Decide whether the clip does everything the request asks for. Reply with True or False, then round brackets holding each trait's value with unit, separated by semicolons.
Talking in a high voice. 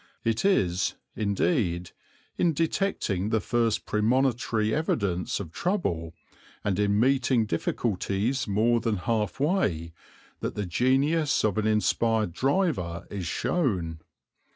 False (110 Hz)